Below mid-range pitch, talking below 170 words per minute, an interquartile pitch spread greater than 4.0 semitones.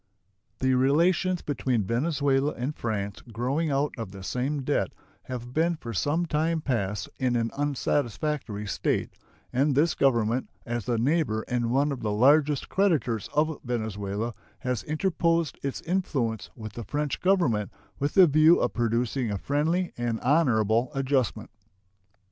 Yes: low, 130 Hz; average, 145 wpm; average, 4.7 semitones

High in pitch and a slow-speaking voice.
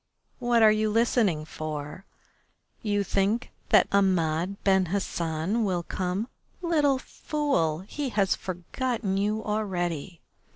Yes: high, 200 Hz; slow, 115 wpm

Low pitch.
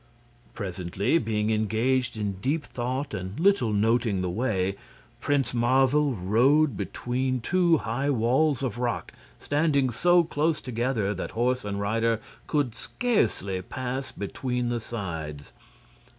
Yes: low, 120 Hz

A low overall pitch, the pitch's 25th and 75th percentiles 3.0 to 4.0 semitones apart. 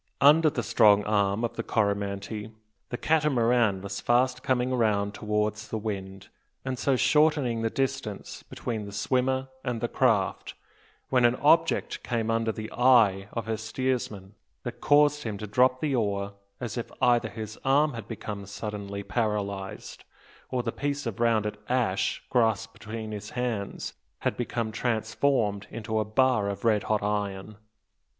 Yes: low, 110 Hz; average, 3.4 semitones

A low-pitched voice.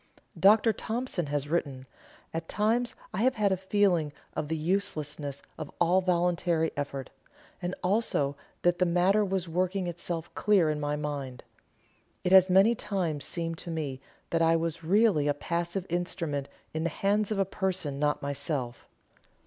No: medium, 170 Hz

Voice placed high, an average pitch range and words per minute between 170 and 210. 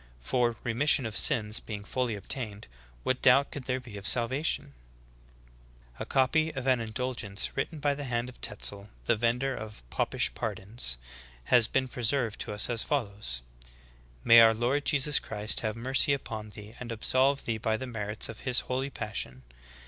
No: low, 120 Hz; average, 3.5 semitones; average, 180 wpm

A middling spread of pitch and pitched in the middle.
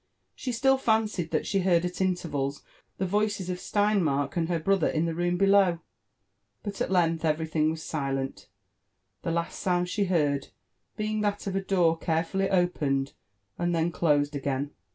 Yes: average, 3.6 semitones; medium, 175 Hz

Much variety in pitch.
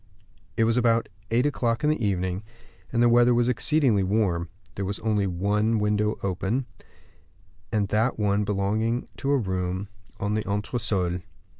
No: average, 3.1 semitones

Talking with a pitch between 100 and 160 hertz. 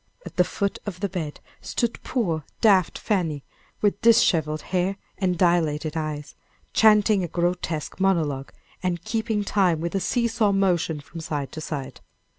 No: medium, 180 Hz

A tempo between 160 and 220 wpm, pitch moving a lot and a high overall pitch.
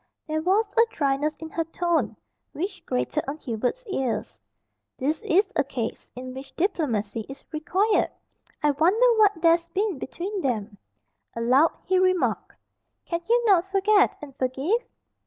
No: average, 145 wpm; wide, 6.4 semitones; very high, 325 Hz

